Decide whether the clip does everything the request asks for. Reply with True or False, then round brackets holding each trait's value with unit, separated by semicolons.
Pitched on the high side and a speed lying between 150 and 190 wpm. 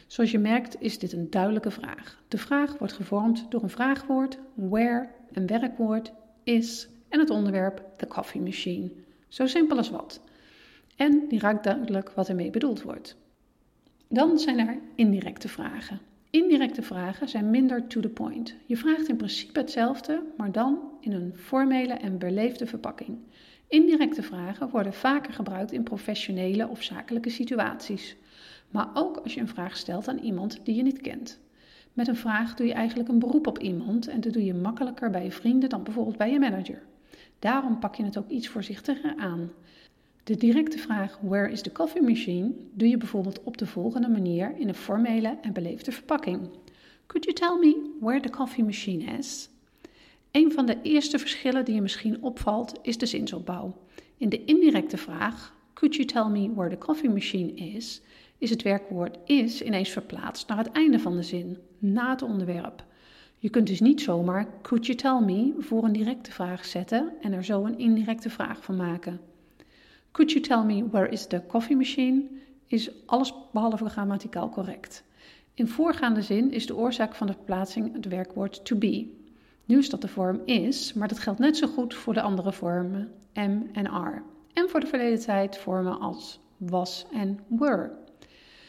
True (230 Hz; 180 wpm)